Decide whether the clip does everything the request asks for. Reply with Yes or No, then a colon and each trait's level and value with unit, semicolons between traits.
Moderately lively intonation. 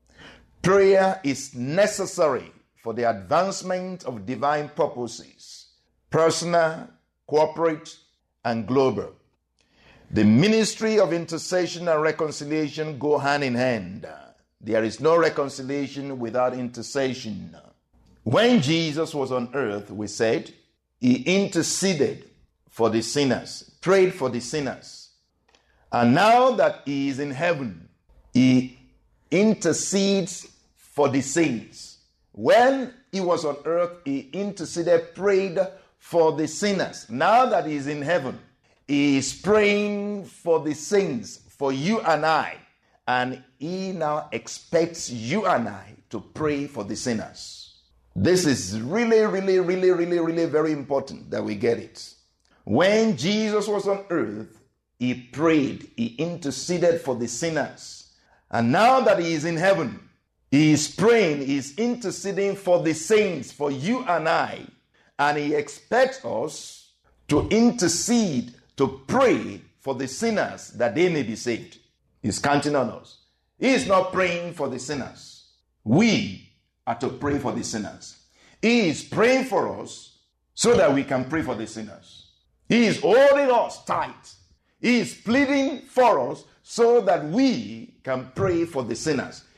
No: wide, 6.8 semitones